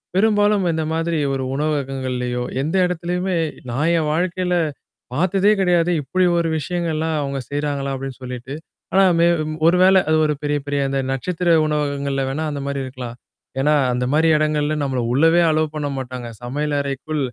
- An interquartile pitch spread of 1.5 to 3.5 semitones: No, average, 3.9 semitones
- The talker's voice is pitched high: No, medium, 150 Hz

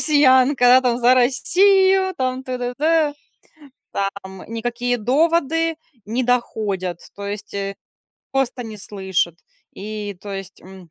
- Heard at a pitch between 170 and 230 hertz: No, high, 245 Hz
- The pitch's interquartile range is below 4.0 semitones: No, average, 5.1 semitones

